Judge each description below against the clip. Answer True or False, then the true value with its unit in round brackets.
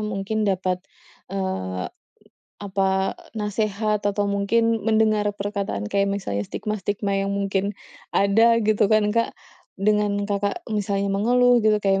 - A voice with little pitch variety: True (1.4 semitones)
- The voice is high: True (205 Hz)